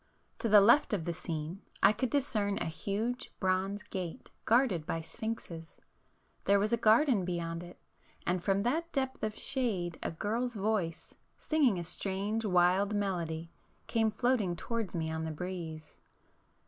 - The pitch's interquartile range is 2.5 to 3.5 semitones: No, average, 4.6 semitones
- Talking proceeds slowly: No, average, 155 wpm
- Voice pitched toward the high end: Yes, high, 200 Hz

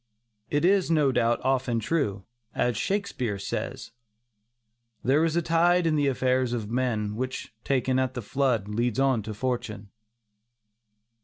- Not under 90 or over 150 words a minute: Yes, average, 145 wpm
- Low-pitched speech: Yes, low, 130 Hz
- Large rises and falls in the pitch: No, average, 4.1 semitones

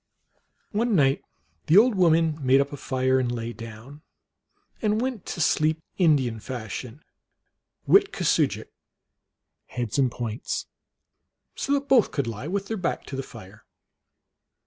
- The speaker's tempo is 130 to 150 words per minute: Yes, average, 140 wpm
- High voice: No, medium, 140 Hz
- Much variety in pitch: Yes, wide, 7.2 semitones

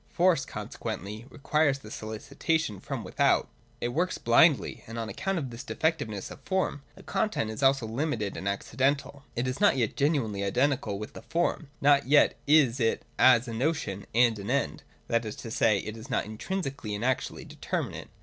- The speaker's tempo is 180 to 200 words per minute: Yes, average, 185 wpm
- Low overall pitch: Yes, low, 130 Hz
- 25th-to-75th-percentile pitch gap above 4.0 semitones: Yes, average, 4.9 semitones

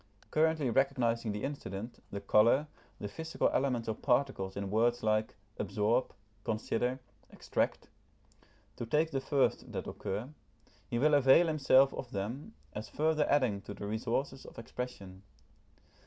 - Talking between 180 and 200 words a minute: No, average, 140 wpm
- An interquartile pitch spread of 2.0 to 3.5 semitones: No, average, 4.4 semitones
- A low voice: Yes, low, 120 Hz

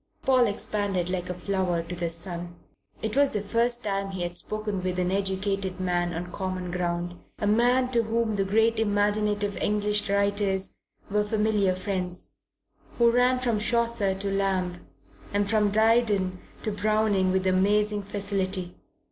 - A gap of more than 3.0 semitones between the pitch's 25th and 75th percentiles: No, narrow, 2.5 semitones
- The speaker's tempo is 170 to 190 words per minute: No, average, 155 wpm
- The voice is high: Yes, high, 200 Hz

